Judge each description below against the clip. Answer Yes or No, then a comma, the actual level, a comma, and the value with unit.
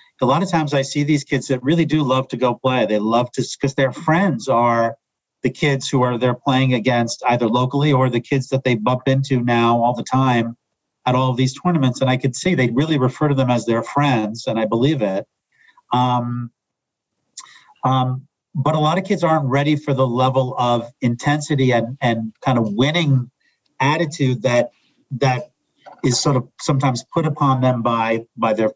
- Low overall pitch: Yes, low, 130 Hz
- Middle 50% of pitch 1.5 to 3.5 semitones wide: Yes, average, 2.8 semitones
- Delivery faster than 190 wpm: Yes, average, 200 wpm